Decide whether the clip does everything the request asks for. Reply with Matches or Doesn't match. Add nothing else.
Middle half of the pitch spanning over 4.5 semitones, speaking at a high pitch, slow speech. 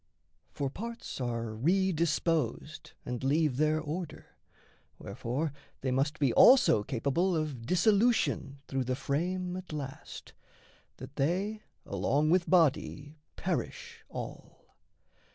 Doesn't match